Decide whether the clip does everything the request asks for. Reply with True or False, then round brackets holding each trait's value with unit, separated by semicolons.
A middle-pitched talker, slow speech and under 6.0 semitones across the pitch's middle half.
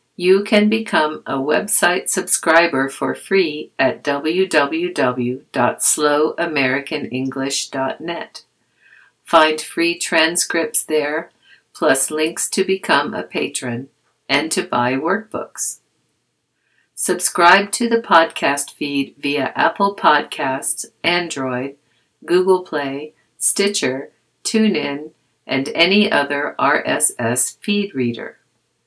True (155 Hz; 90 wpm; 5.6 semitones)